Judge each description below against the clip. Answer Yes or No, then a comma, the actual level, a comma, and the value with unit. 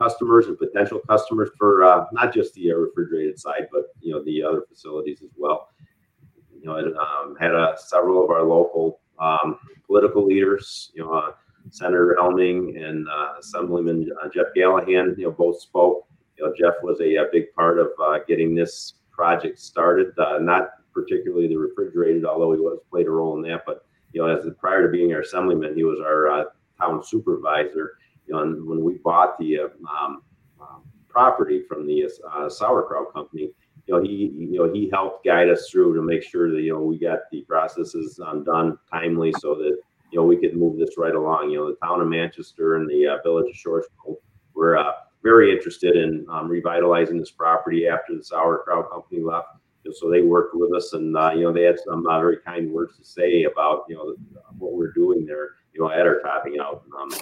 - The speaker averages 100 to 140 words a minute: No, fast, 205 wpm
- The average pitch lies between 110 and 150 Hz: No, very low, 90 Hz